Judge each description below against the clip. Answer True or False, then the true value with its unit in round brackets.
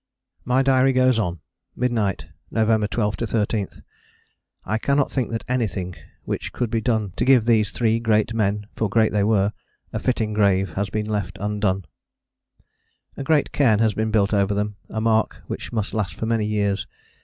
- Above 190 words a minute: False (175 wpm)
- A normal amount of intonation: False (2.1 semitones)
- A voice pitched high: False (110 Hz)